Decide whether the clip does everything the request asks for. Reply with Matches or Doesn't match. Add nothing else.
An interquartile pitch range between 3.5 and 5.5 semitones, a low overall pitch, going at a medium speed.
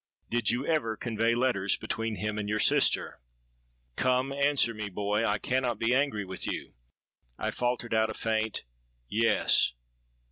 Doesn't match